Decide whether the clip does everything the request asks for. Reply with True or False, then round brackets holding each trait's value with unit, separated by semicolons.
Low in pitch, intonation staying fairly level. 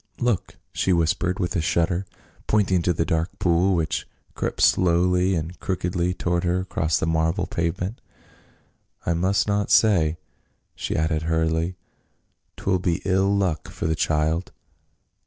True (85 Hz; 2.3 semitones)